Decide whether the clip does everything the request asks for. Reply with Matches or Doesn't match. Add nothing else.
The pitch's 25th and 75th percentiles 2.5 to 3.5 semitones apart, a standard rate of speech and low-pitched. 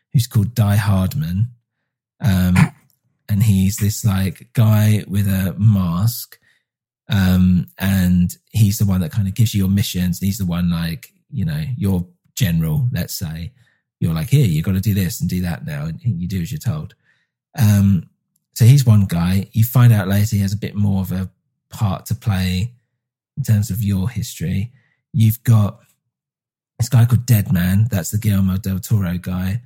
Doesn't match